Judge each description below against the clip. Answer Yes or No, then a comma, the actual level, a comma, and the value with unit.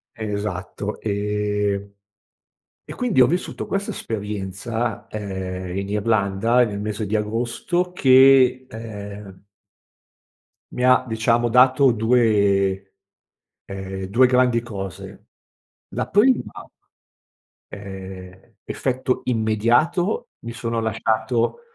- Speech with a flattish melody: No, average, 3.7 semitones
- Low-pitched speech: Yes, low, 110 Hz